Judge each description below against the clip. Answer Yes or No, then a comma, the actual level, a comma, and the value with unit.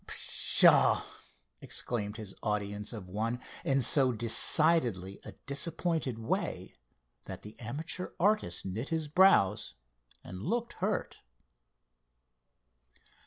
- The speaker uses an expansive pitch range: Yes, wide, 7.7 semitones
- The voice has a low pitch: Yes, low, 120 Hz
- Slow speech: Yes, slow, 100 wpm